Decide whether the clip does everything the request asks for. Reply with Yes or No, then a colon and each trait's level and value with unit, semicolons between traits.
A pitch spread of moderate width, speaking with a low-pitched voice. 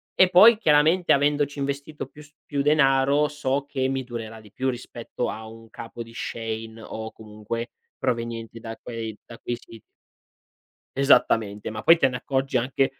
Yes: average, 4.0 semitones; low, 130 Hz